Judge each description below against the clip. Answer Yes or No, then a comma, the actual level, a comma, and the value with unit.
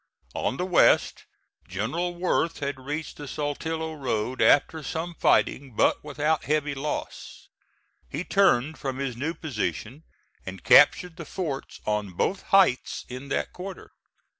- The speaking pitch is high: No, medium, 145 Hz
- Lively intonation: No, average, 4.0 semitones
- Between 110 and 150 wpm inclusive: Yes, average, 140 wpm